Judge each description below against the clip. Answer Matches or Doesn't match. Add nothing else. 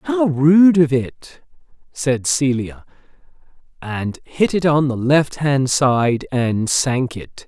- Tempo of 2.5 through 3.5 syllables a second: Matches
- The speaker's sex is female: Doesn't match